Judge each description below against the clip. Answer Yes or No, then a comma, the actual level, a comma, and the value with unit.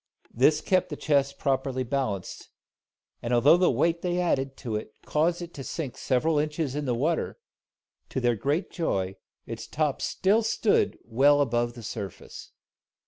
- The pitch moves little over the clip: No, average, 5.1 semitones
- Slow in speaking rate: No, average, 160 wpm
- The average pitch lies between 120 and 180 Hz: Yes, medium, 140 Hz